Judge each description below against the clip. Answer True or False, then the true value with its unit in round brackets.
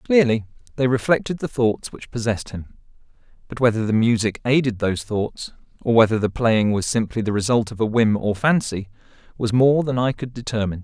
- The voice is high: False (115 Hz)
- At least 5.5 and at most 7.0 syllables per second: True (5.6 syllables/s)